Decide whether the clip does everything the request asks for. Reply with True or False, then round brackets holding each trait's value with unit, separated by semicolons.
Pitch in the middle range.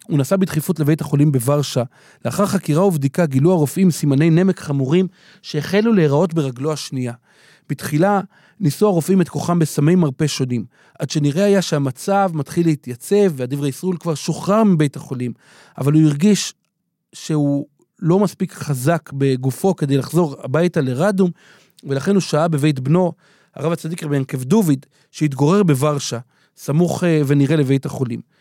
True (155 Hz)